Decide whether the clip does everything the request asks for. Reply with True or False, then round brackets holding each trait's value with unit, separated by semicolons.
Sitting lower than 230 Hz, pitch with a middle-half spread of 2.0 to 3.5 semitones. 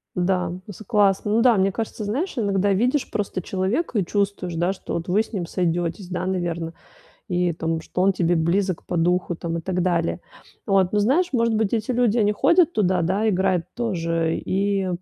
True (190 Hz; 3.2 semitones)